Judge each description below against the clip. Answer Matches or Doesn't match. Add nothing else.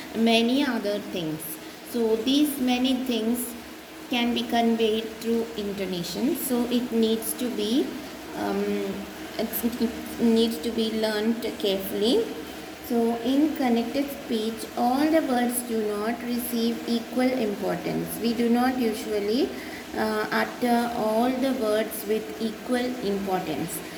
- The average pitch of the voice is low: Doesn't match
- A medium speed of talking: Doesn't match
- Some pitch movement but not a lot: Doesn't match